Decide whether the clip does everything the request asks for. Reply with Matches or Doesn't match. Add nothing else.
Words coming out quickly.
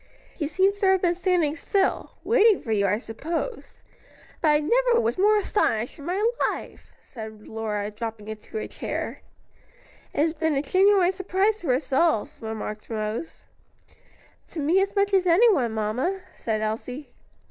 Doesn't match